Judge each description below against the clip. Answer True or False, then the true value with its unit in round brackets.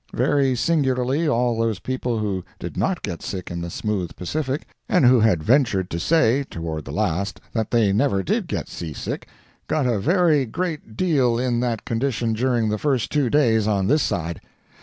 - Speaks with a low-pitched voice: True (120 Hz)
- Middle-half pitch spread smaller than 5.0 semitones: False (5.3 semitones)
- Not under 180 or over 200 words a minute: True (185 wpm)